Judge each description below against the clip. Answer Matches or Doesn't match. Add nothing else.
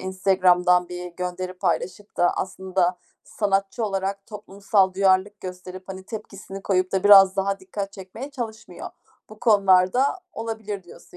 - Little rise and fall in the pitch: Matches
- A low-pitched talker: Doesn't match